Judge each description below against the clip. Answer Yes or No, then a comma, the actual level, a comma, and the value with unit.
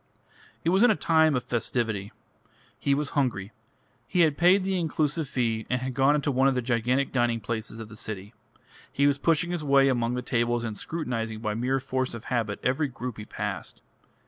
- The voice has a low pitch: Yes, low, 125 Hz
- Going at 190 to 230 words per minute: Yes, average, 200 wpm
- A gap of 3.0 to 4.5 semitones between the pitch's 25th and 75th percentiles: Yes, average, 4.0 semitones